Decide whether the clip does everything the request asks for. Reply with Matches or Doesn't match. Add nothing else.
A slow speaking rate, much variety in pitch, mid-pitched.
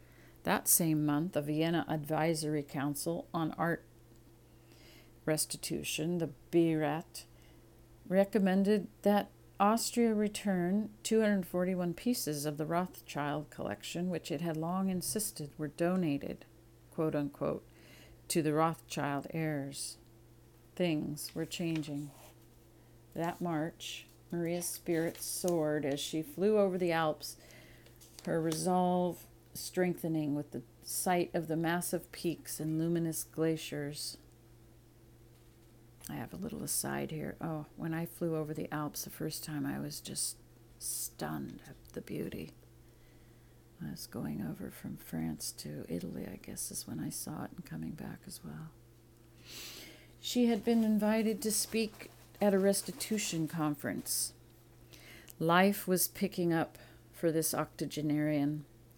Matches